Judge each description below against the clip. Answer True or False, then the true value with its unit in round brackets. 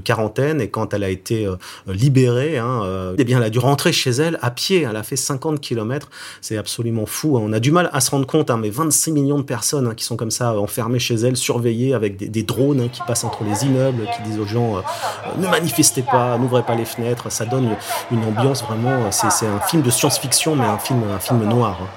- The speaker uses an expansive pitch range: False (3.8 semitones)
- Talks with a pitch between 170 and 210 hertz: False (120 Hz)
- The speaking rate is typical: False (255 wpm)